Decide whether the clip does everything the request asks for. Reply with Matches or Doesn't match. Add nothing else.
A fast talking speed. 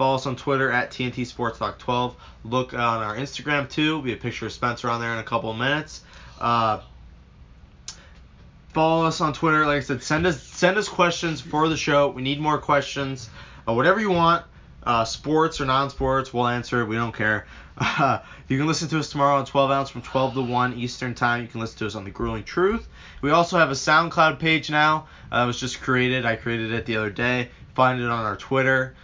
Matches